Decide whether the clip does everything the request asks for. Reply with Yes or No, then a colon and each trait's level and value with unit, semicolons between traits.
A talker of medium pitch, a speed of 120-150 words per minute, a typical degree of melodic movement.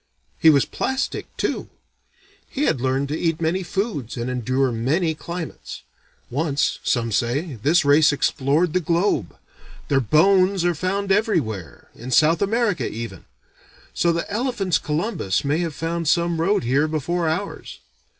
Yes: medium, 160 Hz; average, 145 wpm; average, 5.0 semitones